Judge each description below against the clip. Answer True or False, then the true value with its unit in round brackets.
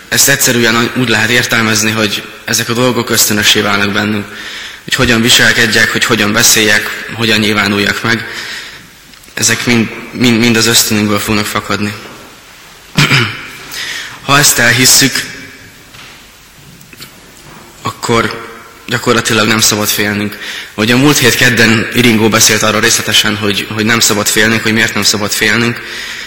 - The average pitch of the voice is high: False (115 Hz)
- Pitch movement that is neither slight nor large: False (1.7 semitones)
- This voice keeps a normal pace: True (130 wpm)